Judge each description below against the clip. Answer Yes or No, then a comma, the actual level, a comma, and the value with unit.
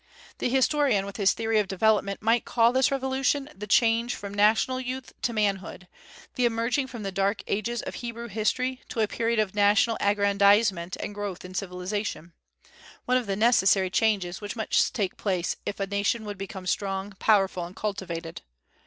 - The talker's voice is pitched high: Yes, high, 210 Hz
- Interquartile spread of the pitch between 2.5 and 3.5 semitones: Yes, average, 3.1 semitones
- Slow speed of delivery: No, average, 175 wpm